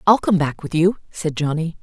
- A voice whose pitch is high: No, medium, 165 Hz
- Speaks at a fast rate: Yes, fast, 230 wpm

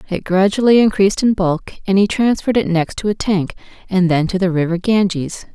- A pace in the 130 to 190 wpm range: No, fast, 205 wpm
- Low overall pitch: No, high, 190 Hz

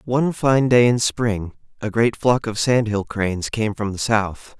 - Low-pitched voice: Yes, low, 110 Hz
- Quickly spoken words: Yes, fast, 210 wpm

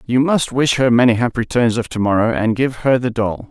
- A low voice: Yes, low, 120 Hz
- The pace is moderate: No, fast, 255 wpm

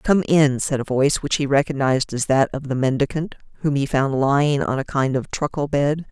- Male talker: No, female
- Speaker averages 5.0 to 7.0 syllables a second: Yes, 5.4 syllables/s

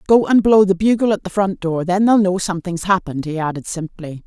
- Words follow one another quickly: Yes, fast, 240 wpm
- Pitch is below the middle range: No, medium, 185 Hz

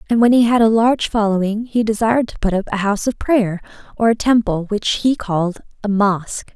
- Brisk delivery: Yes, fast, 220 wpm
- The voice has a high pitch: Yes, high, 215 Hz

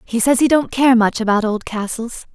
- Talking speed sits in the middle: No, fast, 230 wpm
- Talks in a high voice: Yes, high, 235 Hz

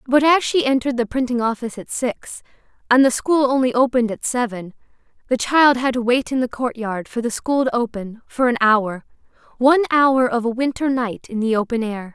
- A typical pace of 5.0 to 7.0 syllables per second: Yes, 5.5 syllables/s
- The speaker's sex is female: Yes, female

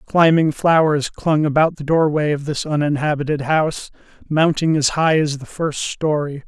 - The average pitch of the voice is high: No, medium, 150 Hz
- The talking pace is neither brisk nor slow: Yes, average, 155 wpm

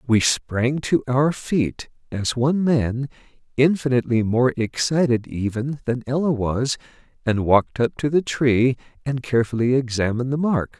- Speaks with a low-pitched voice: Yes, low, 125 Hz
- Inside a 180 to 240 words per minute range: No, average, 145 wpm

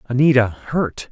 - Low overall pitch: Yes, low, 125 Hz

